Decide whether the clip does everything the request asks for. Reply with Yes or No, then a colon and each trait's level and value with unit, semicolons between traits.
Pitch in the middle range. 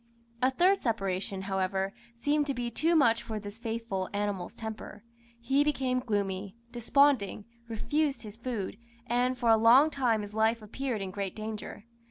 No: high, 225 Hz